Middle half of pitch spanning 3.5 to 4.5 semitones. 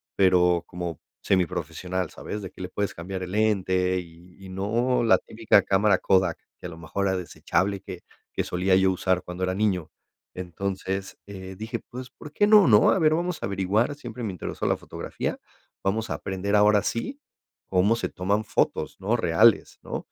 No: average, 2.8 semitones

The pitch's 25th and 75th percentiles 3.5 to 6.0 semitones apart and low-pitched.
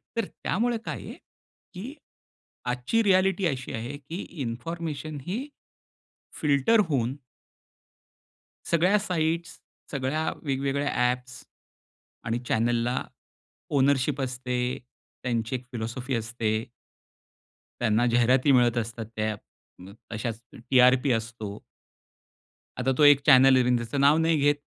Yes: average, 4.6 semitones; low, 130 Hz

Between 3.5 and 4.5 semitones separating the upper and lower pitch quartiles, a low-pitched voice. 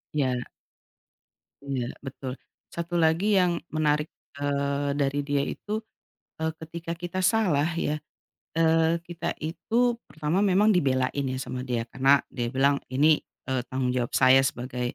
No: average, 3.8 semitones; medium, 145 Hz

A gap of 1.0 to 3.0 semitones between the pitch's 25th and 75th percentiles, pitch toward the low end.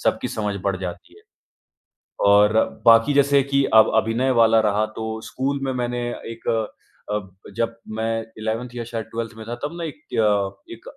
Yes: narrow, 2.5 semitones; low, 115 Hz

